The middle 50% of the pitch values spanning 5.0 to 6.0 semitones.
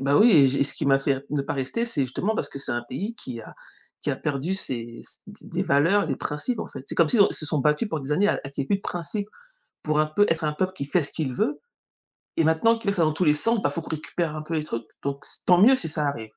Yes: wide, 5.6 semitones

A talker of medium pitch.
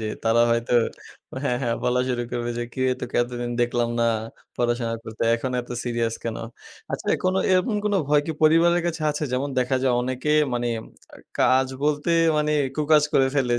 No: low, 125 Hz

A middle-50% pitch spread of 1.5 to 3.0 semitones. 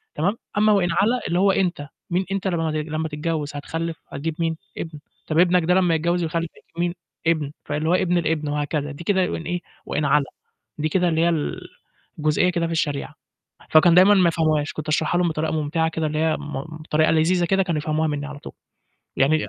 Yes: narrow, 2.4 semitones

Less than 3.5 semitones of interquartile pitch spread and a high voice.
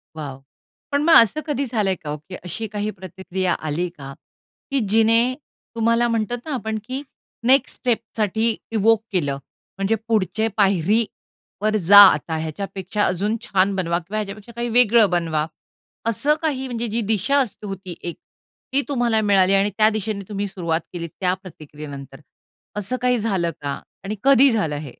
No: average, 4.3 semitones; high, 205 Hz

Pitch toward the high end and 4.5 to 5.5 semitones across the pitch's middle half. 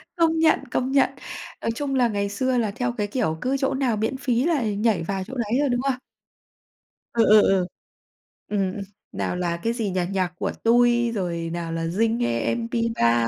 Yes: high, 225 Hz; average, 4.8 semitones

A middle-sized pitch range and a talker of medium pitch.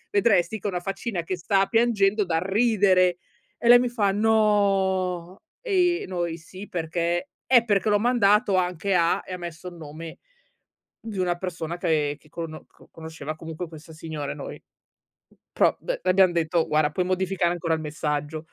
Yes: average, 3.8 semitones; medium, 180 Hz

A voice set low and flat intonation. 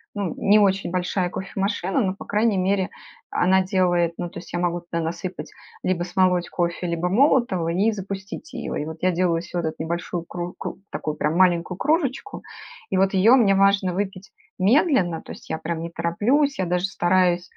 No: medium, 185 Hz; narrow, 2.3 semitones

